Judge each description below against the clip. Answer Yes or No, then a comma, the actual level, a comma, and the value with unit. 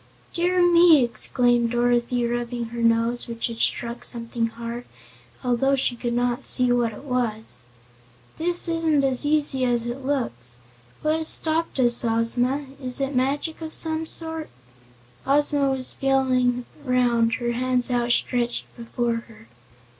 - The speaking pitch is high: Yes, high, 245 Hz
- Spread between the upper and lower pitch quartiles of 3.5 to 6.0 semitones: No, average, 2.9 semitones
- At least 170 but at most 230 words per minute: No, average, 140 wpm